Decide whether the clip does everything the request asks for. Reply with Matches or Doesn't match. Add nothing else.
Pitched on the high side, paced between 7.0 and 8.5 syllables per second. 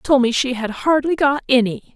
Doesn't match